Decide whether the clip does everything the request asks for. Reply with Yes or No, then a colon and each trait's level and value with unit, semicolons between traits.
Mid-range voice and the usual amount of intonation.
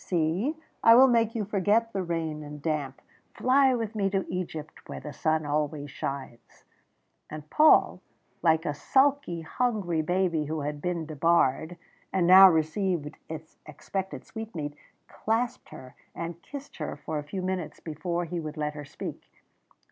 Yes: medium, 170 Hz; average, 4.6 semitones